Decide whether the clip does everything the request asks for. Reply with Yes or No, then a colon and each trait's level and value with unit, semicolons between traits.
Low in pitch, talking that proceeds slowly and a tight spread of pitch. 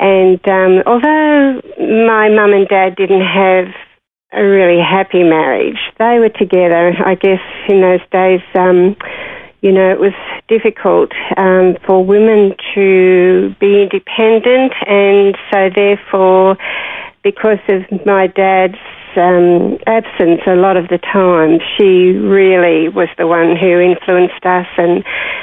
No: high, 190 Hz; slow, 130 wpm; narrow, 1.8 semitones